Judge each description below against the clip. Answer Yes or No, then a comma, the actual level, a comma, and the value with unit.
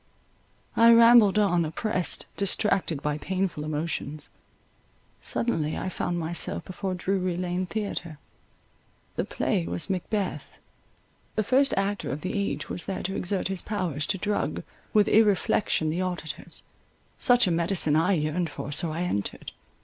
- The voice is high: No, medium, 180 Hz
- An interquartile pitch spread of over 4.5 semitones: No, average, 3.9 semitones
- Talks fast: No, slow, 135 wpm